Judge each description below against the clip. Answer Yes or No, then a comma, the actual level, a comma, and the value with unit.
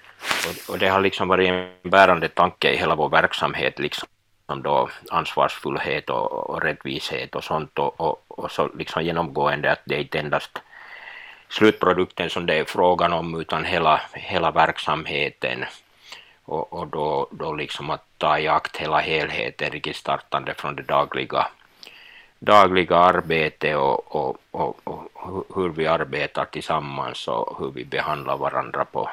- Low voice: Yes, very low, 90 Hz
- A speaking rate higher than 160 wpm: No, average, 145 wpm